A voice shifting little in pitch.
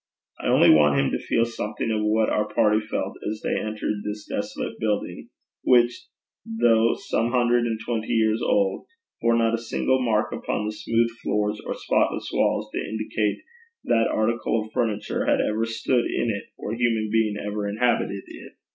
Yes: narrow, 1.6 semitones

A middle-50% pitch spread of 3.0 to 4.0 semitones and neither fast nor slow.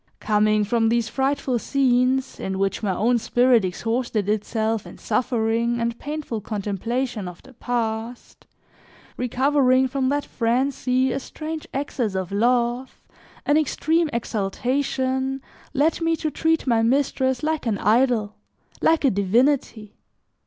No: average, 3.4 semitones; slow, 130 wpm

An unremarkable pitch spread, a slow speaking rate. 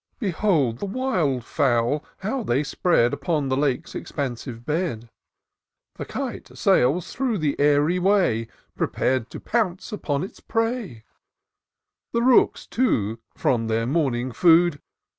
No: wide, 7.3 semitones; slow, 125 wpm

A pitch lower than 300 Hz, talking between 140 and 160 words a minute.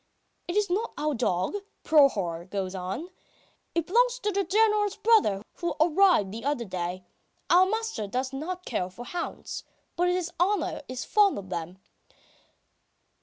No: very high, 320 Hz; average, 150 wpm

